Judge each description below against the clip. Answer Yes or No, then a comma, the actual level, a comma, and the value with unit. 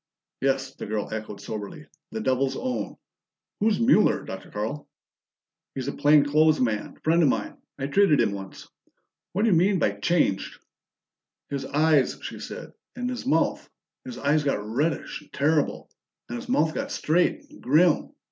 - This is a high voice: No, medium, 145 Hz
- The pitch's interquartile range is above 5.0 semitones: Yes, wide, 5.6 semitones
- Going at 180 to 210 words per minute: No, average, 165 wpm